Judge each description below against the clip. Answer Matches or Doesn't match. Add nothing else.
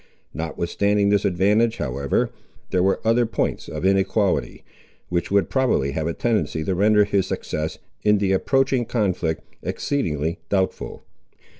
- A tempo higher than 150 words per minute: Doesn't match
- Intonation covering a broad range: Doesn't match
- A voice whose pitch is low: Matches